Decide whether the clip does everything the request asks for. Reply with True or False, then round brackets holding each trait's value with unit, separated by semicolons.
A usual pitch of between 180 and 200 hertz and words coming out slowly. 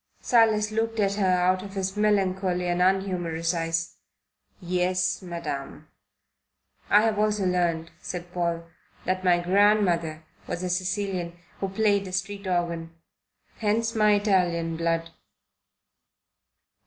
True (185 Hz; 120 wpm)